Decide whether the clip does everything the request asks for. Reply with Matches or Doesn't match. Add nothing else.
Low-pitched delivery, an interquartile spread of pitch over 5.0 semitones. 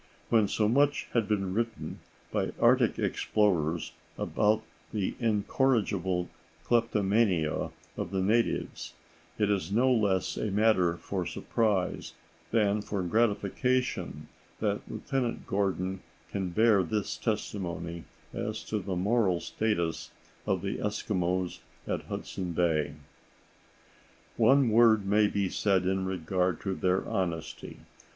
Doesn't match